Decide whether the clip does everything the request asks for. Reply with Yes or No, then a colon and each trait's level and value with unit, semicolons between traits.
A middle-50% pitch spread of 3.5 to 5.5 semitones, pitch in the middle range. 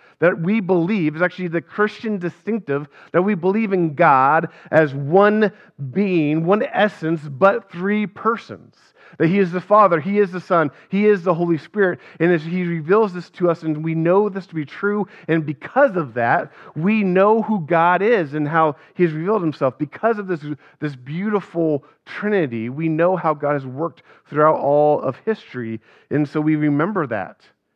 Yes: average, 4.5 semitones; medium, 175 Hz